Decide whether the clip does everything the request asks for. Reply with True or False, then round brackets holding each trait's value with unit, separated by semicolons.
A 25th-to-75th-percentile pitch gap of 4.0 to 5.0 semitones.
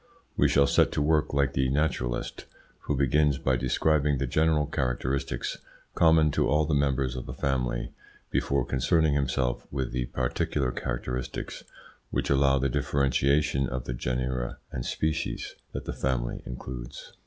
False (2.4 semitones)